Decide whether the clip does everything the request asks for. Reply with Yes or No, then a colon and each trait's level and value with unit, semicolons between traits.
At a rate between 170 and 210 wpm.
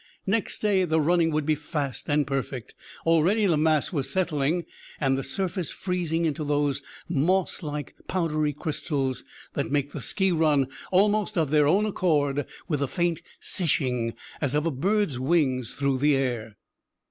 No: average, 160 wpm